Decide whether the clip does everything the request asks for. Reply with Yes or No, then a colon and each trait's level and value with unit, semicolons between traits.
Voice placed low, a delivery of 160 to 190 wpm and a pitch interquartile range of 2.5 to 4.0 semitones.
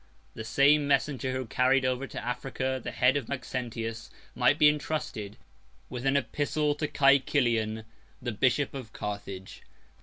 No: low, 130 Hz; average, 140 wpm; average, 3.6 semitones